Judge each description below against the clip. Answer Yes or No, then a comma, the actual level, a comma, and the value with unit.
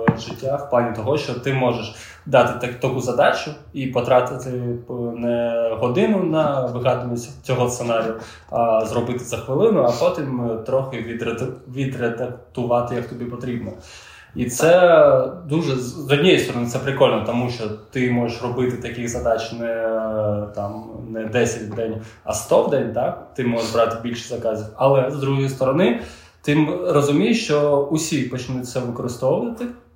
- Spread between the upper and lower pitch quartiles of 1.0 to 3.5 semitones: Yes, narrow, 2.5 semitones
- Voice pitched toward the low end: Yes, low, 120 Hz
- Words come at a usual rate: Yes, average, 145 wpm